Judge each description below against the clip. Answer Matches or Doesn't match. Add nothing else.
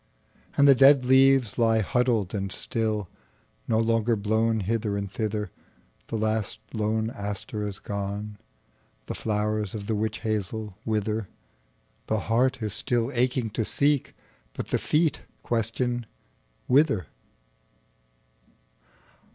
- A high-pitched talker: Doesn't match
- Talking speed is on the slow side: Matches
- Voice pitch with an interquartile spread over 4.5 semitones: Doesn't match